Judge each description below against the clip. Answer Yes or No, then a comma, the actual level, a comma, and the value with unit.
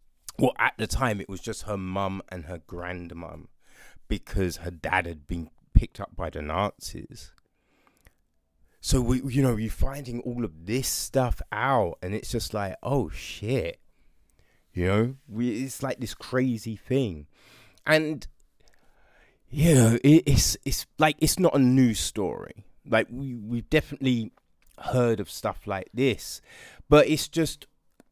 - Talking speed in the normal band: Yes, average, 155 wpm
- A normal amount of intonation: No, wide, 6.5 semitones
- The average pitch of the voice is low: Yes, low, 115 Hz